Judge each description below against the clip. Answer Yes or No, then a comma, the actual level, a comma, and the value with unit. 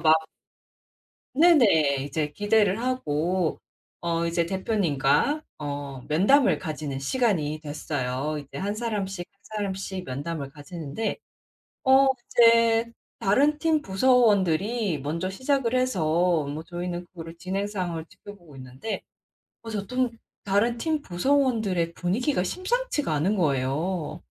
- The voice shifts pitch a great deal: Yes, wide, 6.8 semitones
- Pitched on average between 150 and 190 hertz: Yes, medium, 185 Hz